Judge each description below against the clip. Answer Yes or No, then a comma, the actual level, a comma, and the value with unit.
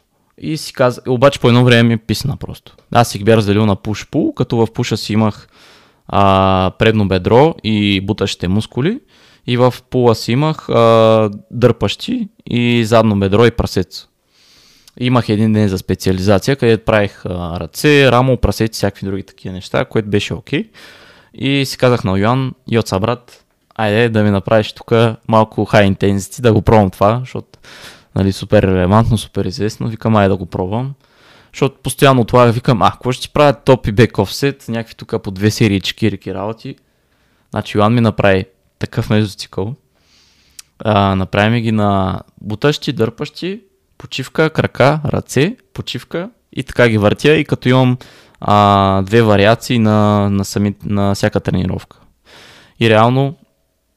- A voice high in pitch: No, low, 110 Hz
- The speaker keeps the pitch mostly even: No, average, 3.7 semitones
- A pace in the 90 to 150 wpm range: No, average, 160 wpm